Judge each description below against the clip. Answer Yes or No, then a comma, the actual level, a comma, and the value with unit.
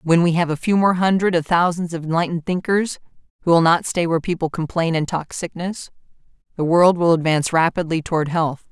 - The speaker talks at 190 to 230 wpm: Yes, average, 200 wpm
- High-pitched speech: No, medium, 170 Hz